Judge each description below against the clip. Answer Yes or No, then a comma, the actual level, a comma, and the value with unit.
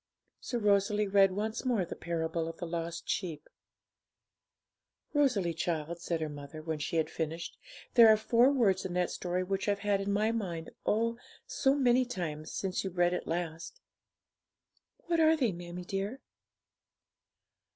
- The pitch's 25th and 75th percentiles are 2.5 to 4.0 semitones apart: No, average, 4.6 semitones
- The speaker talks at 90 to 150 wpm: No, average, 160 wpm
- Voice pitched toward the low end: No, high, 190 Hz